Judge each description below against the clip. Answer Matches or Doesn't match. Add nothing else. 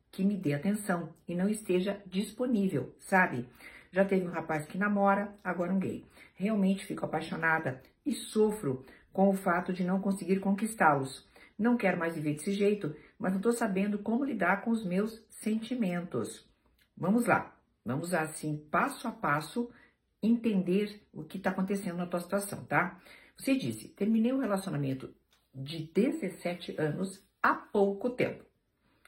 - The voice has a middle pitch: Doesn't match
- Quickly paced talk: Doesn't match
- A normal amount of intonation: Matches